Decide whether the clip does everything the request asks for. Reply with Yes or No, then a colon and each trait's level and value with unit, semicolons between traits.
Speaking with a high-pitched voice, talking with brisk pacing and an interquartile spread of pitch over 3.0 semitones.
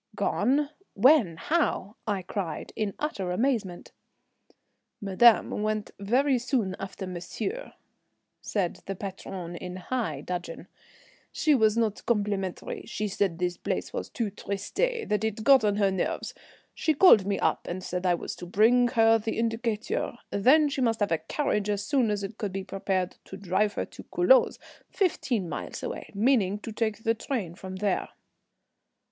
No: high, 210 Hz; average, 160 wpm; average, 4.0 semitones